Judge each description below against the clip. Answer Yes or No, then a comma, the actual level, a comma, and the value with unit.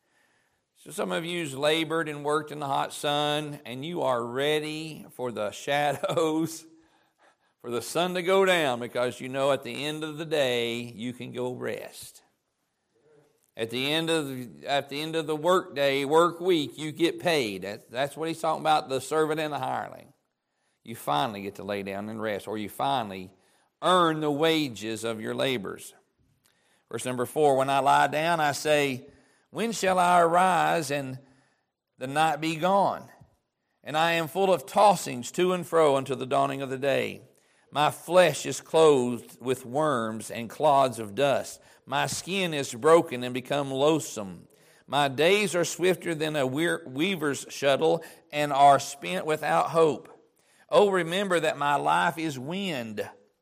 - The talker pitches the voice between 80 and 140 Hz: No, medium, 150 Hz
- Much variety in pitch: No, average, 3.7 semitones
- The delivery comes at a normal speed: Yes, average, 170 wpm